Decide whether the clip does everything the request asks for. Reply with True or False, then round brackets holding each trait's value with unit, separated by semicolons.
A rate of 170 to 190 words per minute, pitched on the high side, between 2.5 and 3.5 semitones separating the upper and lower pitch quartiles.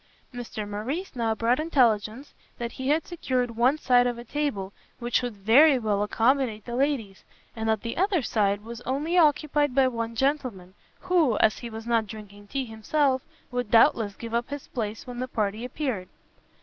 False (180 wpm; 240 Hz; 3.9 semitones)